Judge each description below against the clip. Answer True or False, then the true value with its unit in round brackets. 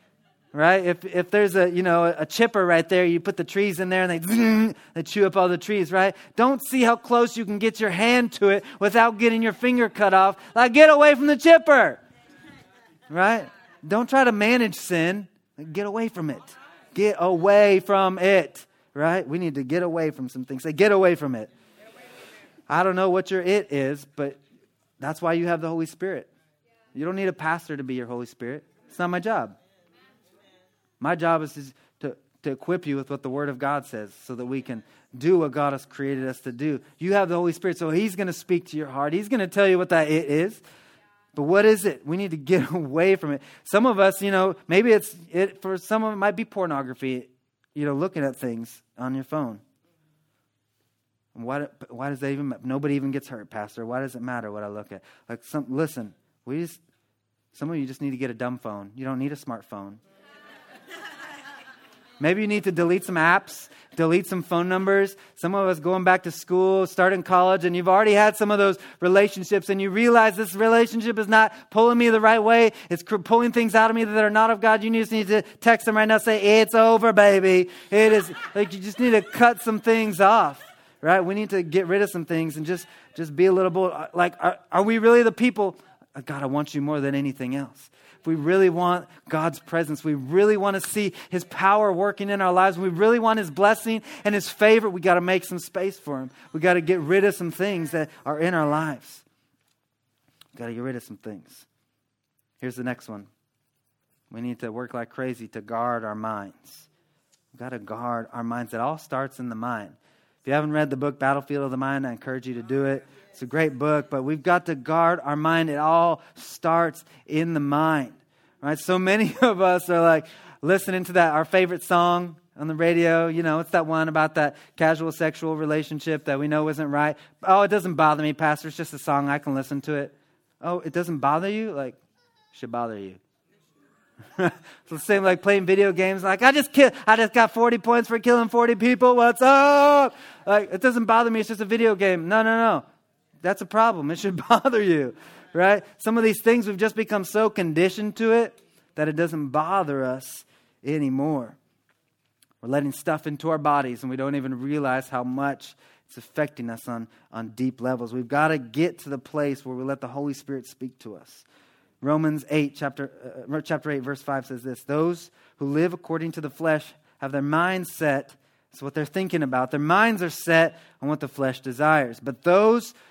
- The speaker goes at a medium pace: False (220 wpm)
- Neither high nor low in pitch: True (170 Hz)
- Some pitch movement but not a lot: False (6.0 semitones)